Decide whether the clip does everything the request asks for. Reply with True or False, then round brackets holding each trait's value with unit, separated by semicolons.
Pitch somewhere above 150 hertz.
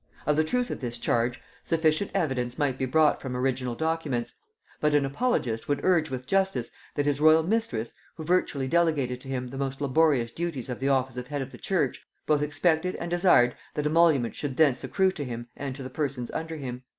False (140 Hz)